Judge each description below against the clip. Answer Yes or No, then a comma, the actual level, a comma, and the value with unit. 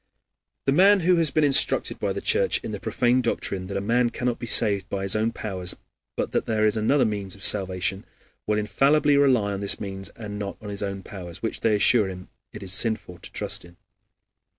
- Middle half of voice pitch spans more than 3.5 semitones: Yes, average, 4.2 semitones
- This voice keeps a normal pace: No, fast, 220 wpm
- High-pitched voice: No, low, 105 Hz